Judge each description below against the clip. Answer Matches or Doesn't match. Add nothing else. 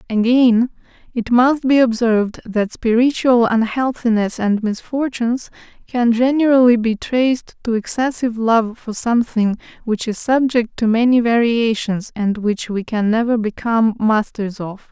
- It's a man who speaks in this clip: Doesn't match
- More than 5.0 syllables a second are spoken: Doesn't match